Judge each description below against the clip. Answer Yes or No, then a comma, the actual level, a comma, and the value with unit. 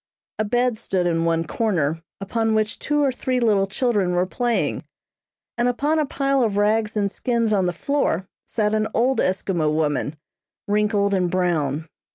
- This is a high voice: Yes, high, 210 Hz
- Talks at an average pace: Yes, average, 170 wpm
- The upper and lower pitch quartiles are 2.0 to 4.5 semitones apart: No, average, 5.1 semitones